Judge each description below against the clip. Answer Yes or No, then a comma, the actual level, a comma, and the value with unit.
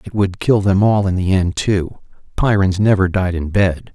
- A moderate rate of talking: No, fast, 215 wpm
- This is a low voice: Yes, very low, 95 Hz